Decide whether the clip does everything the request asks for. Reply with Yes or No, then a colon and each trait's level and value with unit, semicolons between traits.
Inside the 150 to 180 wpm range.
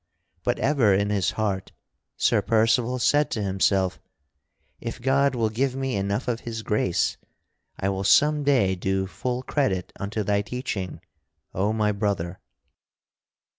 No: average, 140 wpm